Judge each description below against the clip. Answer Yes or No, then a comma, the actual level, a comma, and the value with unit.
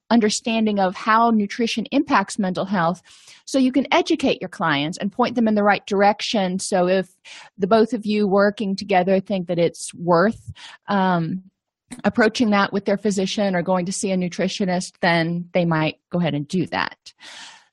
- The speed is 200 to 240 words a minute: No, average, 175 wpm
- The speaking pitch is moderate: No, high, 200 Hz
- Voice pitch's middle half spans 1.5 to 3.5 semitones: Yes, average, 3.2 semitones